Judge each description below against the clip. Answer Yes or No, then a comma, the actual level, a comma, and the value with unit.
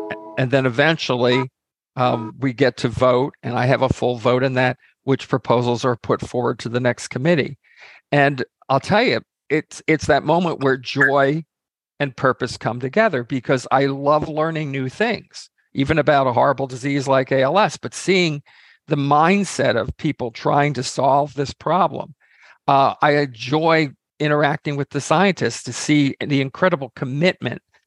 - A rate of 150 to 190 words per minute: Yes, average, 160 wpm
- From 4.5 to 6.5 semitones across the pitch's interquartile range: No, average, 2.9 semitones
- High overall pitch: No, low, 135 Hz